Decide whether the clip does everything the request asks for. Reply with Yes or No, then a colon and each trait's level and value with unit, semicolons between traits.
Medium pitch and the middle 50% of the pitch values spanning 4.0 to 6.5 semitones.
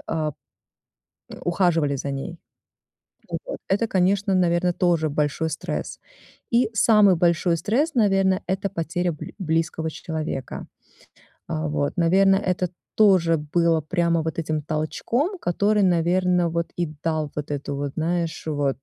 No: medium, 170 Hz; average, 3.2 semitones